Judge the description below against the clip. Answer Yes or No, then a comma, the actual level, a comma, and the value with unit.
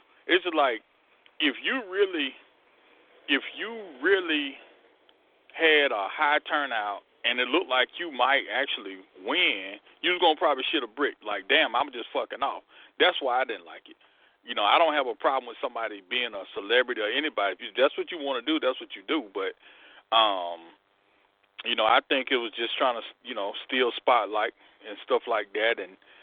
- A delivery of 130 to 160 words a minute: No, average, 190 wpm